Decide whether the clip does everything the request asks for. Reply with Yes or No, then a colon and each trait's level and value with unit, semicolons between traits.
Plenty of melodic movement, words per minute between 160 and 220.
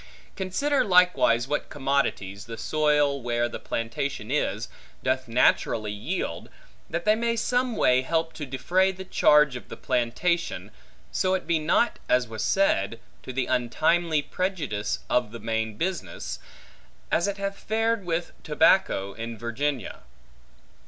No: wide, 7.5 semitones; average, 140 wpm